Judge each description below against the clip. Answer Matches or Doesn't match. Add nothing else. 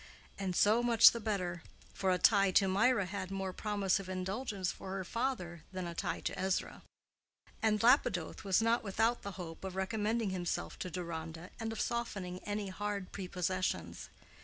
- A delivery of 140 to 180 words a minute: Matches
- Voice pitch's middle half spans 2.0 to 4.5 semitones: Matches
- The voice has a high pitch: Matches